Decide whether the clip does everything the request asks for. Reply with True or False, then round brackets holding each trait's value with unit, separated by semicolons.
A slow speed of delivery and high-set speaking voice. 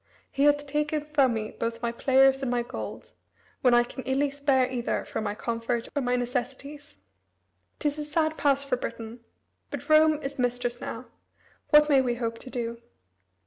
False (185 wpm; 260 Hz)